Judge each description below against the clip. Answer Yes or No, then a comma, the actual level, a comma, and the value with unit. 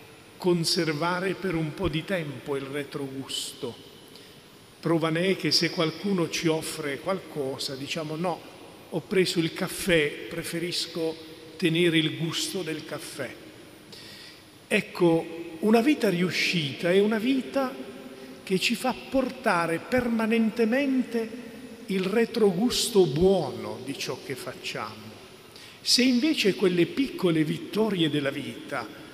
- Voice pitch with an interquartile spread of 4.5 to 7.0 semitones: Yes, average, 4.9 semitones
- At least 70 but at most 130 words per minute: Yes, slow, 115 wpm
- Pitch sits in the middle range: Yes, medium, 175 Hz